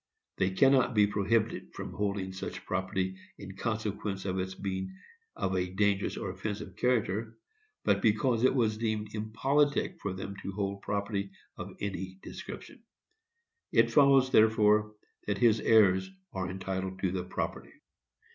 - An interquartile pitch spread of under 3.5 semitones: Yes, narrow, 2.6 semitones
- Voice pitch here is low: Yes, low, 100 Hz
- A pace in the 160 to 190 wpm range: No, average, 145 wpm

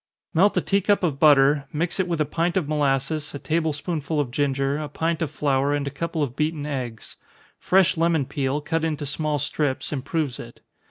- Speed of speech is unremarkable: No, fast, 210 wpm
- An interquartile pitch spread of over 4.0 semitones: No, average, 2.7 semitones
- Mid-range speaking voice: Yes, medium, 150 Hz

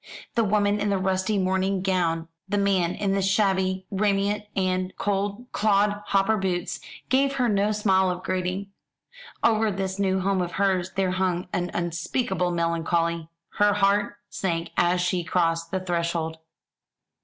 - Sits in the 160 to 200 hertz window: Yes, high, 190 Hz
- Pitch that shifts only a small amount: Yes, narrow, 2.2 semitones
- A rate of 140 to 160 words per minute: Yes, average, 145 wpm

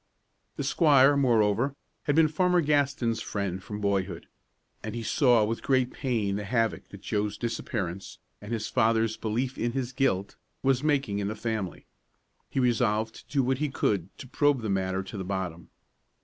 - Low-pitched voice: Yes, low, 115 Hz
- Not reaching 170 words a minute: No, average, 175 wpm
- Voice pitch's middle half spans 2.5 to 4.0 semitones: No, average, 4.7 semitones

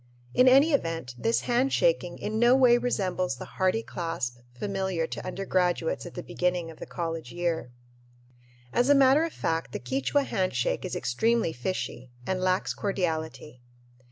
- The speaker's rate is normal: Yes, average, 155 wpm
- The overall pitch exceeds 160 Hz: Yes, medium, 185 Hz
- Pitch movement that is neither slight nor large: No, wide, 6.6 semitones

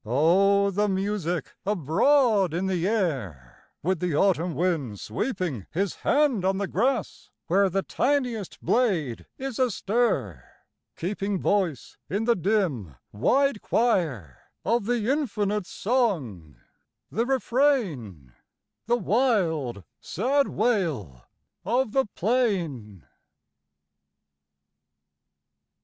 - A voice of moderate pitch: No, high, 195 Hz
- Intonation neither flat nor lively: No, wide, 7.1 semitones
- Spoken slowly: Yes, slow, 100 wpm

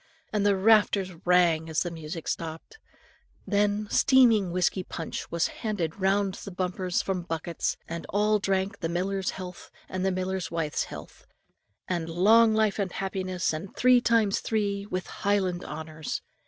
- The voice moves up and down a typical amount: Yes, average, 3.0 semitones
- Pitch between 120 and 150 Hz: No, high, 190 Hz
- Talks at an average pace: Yes, average, 155 wpm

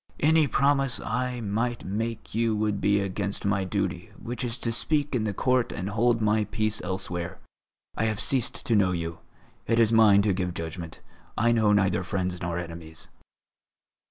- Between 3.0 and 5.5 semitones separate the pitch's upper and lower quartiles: Yes, average, 3.9 semitones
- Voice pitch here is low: Yes, low, 105 Hz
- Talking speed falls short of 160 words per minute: No, average, 175 wpm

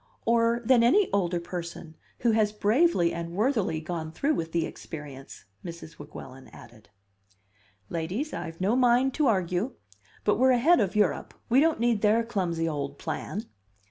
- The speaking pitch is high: Yes, high, 200 Hz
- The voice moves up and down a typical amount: No, wide, 6.3 semitones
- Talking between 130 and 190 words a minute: Yes, average, 155 wpm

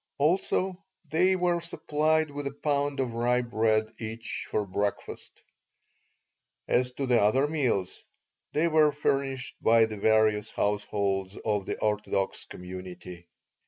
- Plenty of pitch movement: Yes, wide, 5.9 semitones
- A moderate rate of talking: No, slow, 125 wpm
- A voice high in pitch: No, low, 120 Hz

